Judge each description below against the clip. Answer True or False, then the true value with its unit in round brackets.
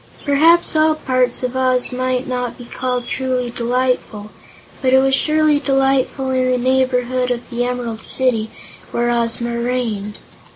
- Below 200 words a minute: True (150 wpm)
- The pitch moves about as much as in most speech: False (1.5 semitones)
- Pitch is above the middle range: True (255 Hz)